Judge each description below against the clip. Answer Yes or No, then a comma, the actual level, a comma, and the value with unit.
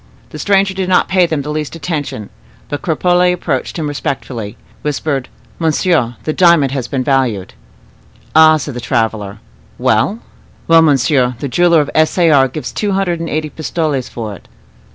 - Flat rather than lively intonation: No, average, 4.6 semitones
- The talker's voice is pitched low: No, medium, 150 Hz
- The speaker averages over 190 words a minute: No, average, 170 wpm